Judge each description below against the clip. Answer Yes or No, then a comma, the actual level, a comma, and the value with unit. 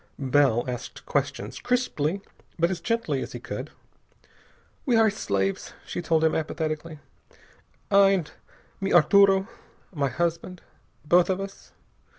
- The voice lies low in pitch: No, medium, 170 Hz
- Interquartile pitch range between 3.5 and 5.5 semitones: Yes, average, 4.6 semitones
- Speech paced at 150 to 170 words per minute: No, slow, 135 wpm